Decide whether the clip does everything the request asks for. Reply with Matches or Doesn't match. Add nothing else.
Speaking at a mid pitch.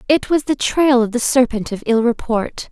Doesn't match